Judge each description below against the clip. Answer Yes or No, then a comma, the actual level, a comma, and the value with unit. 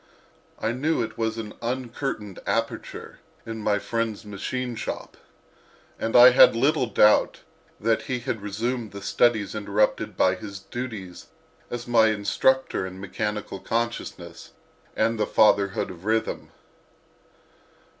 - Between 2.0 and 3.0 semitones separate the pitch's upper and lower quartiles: Yes, average, 2.7 semitones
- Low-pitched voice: Yes, low, 110 Hz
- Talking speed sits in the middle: No, slow, 125 wpm